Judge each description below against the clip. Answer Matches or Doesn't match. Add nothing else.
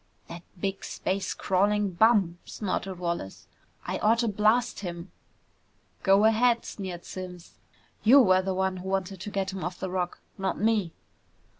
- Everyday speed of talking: Matches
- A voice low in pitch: Doesn't match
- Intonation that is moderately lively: Doesn't match